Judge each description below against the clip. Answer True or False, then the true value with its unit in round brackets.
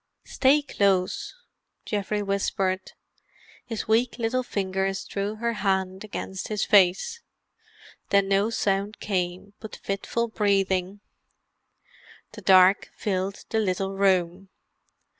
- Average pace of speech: False (105 wpm)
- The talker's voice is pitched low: False (195 Hz)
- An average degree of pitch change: False (2.0 semitones)